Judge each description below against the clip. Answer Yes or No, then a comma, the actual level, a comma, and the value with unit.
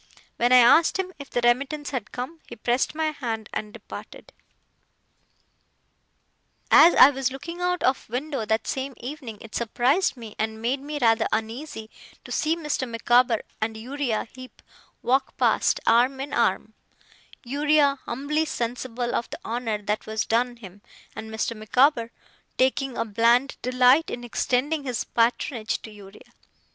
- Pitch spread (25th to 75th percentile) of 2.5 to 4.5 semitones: Yes, average, 3.7 semitones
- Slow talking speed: No, average, 155 wpm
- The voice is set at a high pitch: Yes, very high, 250 Hz